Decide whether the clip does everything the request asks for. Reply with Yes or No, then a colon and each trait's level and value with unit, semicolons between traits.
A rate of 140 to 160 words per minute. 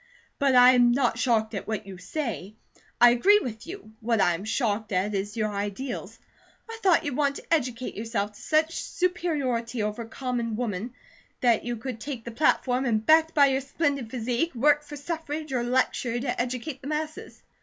No: average, 185 wpm